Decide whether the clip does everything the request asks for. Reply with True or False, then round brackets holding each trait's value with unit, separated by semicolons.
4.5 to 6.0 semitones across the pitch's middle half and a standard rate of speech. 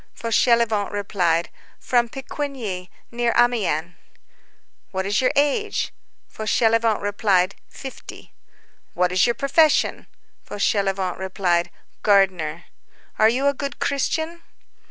False (5.2 semitones; 100 wpm)